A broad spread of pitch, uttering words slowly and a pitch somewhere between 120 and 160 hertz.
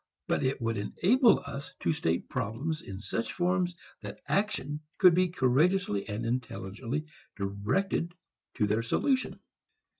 Yes: wide, 8.8 semitones; slow, 130 wpm; low, 135 Hz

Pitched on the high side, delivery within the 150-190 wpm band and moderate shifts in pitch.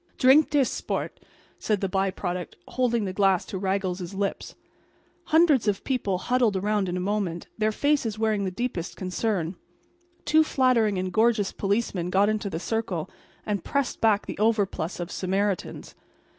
Yes: high, 205 Hz; average, 155 wpm; average, 3.5 semitones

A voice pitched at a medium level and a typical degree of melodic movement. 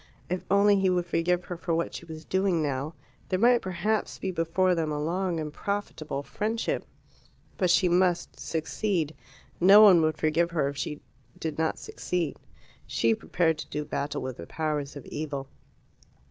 Yes: medium, 165 Hz; average, 3.4 semitones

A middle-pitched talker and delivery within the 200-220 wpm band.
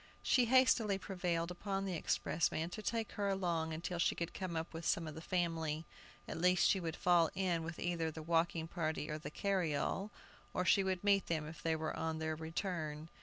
Yes: medium, 170 Hz; fast, 205 wpm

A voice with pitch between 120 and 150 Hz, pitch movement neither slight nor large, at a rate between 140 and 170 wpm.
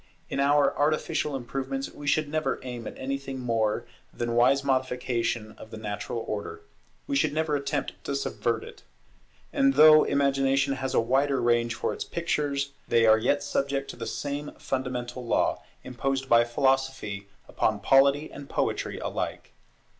Yes: low, 135 Hz; average, 3.0 semitones; average, 155 wpm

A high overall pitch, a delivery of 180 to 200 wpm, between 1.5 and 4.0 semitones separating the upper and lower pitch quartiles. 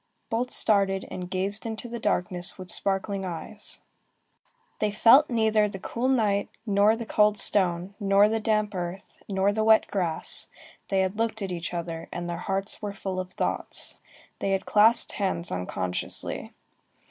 No: high, 200 Hz; average, 160 wpm; average, 2.7 semitones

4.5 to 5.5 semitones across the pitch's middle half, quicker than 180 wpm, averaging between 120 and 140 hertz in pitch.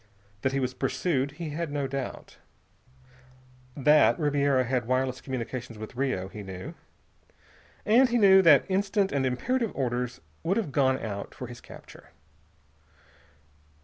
No: average, 5.0 semitones; average, 140 wpm; low, 135 Hz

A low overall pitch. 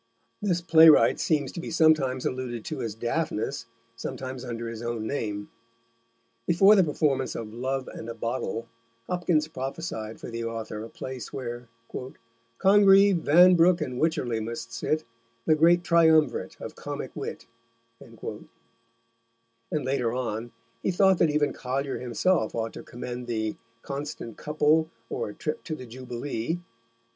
Yes: low, 130 Hz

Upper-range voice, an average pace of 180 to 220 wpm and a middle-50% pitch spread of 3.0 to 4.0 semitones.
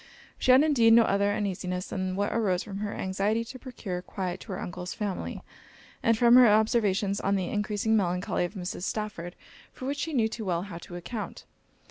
Yes: high, 205 Hz; average, 195 wpm; average, 3.5 semitones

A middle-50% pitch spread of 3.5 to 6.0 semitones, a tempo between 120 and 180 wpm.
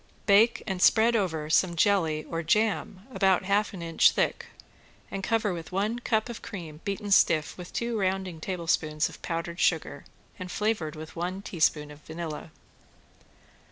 Yes: average, 3.9 semitones; average, 160 wpm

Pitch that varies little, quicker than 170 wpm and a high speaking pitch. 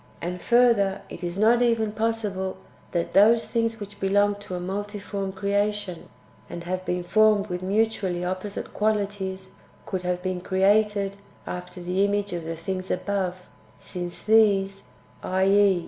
No: narrow, 2.2 semitones; average, 145 wpm; high, 195 Hz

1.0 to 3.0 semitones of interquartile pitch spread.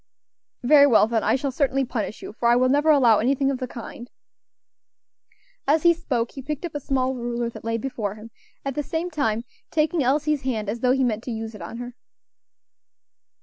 No: average, 3.6 semitones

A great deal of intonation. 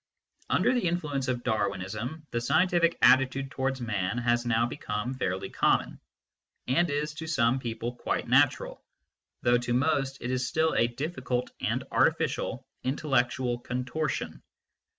No: average, 3.5 semitones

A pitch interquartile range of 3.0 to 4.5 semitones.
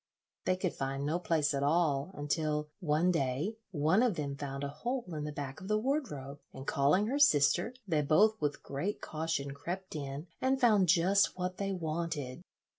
No: average, 4.9 semitones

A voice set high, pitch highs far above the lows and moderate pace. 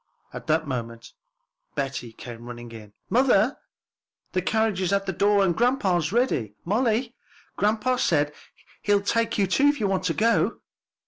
Yes: high, 195 Hz; wide, 8.2 semitones; average, 155 wpm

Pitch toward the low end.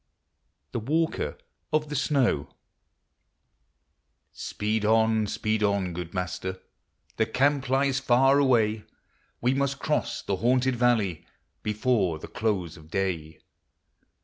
Yes: low, 110 Hz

